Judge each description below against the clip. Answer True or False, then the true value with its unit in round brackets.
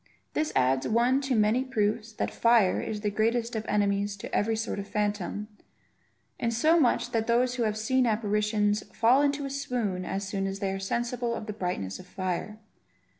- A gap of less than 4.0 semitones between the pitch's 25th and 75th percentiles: True (2.9 semitones)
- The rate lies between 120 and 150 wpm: False (195 wpm)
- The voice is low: False (215 Hz)